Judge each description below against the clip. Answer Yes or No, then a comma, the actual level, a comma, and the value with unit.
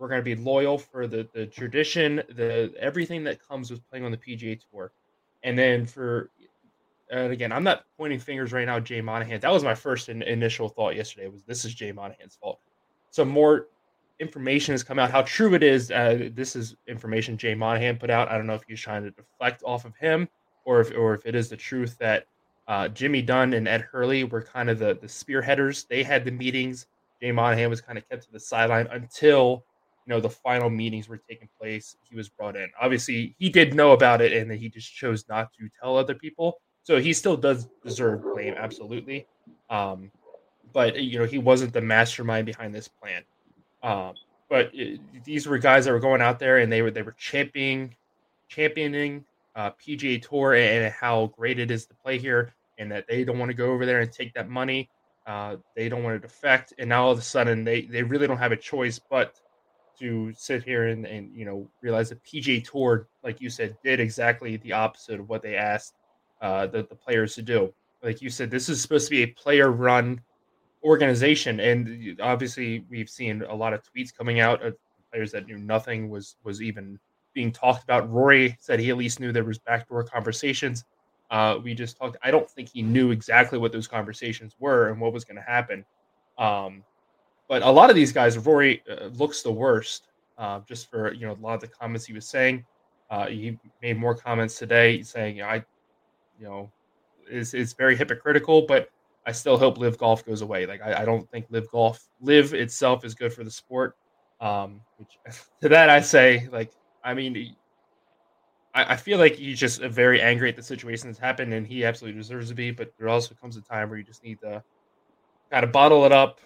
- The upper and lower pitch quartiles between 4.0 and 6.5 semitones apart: No, narrow, 2.5 semitones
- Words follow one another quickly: Yes, fast, 215 wpm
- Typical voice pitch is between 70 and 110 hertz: No, low, 120 Hz